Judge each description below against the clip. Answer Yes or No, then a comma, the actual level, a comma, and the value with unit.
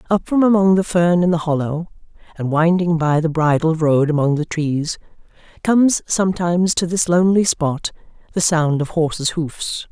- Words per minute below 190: Yes, average, 170 wpm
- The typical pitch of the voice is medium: Yes, medium, 165 Hz